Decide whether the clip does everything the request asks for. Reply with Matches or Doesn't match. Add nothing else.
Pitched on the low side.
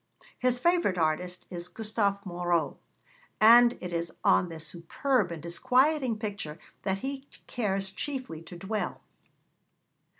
Doesn't match